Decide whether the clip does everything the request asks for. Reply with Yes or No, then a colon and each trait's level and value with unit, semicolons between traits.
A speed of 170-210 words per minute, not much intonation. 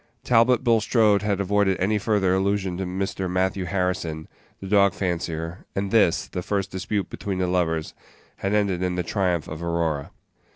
Yes: average, 175 wpm; narrow, 2.3 semitones